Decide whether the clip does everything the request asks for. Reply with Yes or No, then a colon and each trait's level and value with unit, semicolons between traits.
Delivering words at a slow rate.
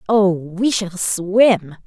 Yes: slow, 130 wpm